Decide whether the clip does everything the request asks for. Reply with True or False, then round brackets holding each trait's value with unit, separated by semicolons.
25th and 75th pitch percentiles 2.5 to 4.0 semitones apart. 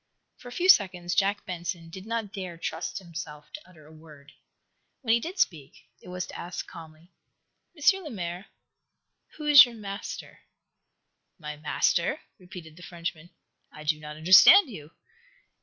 False (5.1 semitones)